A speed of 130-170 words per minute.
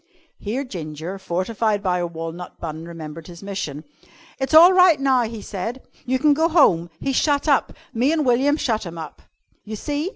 No: average, 185 wpm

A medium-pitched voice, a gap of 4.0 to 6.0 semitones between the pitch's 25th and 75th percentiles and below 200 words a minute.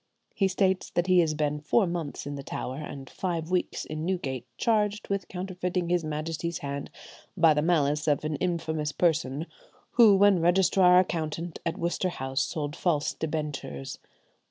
No: medium, 165 Hz; average, 3.4 semitones; average, 160 wpm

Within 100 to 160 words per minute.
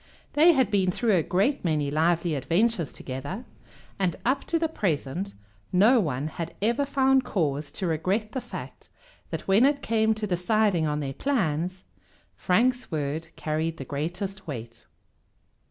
Yes: average, 155 wpm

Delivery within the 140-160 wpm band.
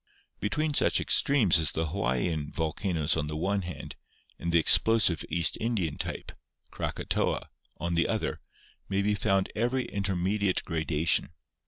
Yes: average, 150 wpm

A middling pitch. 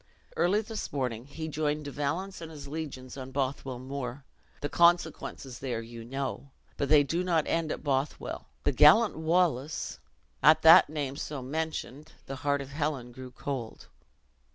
Yes: medium, 145 Hz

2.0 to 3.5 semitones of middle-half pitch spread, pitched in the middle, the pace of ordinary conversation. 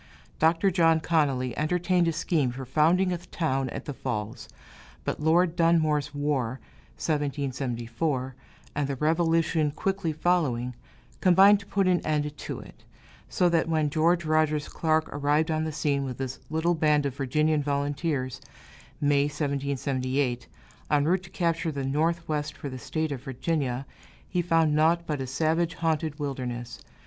Yes: average, 3.1 semitones; medium, 150 Hz; average, 150 wpm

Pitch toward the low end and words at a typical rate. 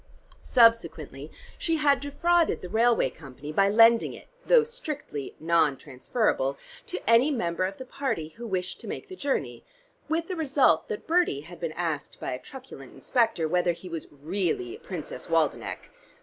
No: high, 220 Hz; average, 165 wpm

